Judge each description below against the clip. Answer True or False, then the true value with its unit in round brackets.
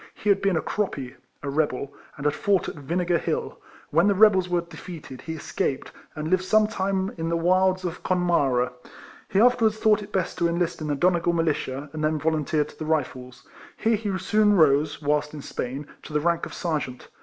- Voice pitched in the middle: True (170 Hz)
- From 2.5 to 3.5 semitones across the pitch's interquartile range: False (4.1 semitones)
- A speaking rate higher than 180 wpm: True (200 wpm)